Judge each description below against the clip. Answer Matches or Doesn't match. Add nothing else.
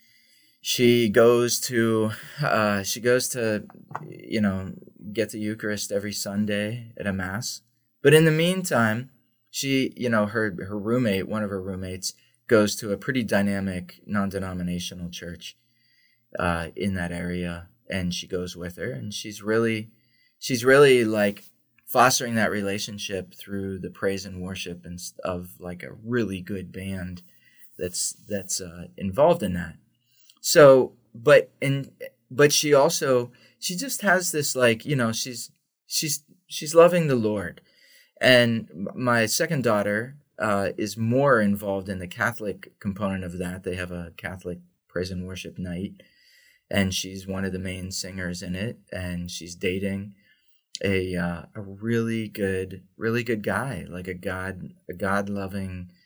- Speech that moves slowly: Doesn't match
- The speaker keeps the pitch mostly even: Doesn't match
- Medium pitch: Doesn't match